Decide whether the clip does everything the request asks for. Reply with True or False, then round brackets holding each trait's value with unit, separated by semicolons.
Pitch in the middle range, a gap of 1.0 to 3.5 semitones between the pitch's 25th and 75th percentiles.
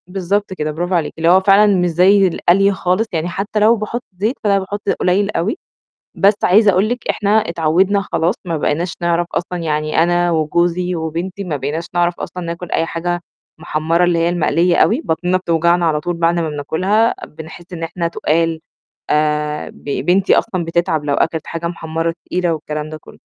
True (175 Hz; 2.6 semitones)